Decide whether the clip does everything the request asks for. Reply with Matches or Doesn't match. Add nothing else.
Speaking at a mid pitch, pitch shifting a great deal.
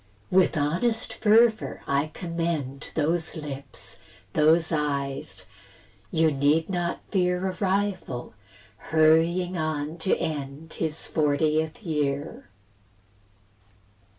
Doesn't match